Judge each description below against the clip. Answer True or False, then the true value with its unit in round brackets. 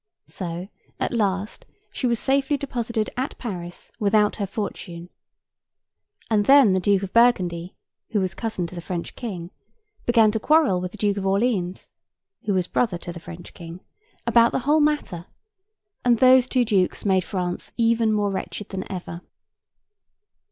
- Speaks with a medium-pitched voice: False (205 Hz)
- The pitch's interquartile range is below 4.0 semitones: False (4.6 semitones)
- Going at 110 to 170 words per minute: True (160 wpm)